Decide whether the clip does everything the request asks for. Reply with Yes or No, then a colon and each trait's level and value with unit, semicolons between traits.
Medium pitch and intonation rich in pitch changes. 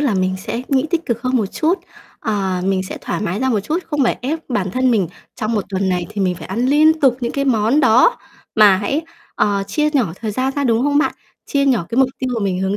No: high, 230 Hz; wide, 5.7 semitones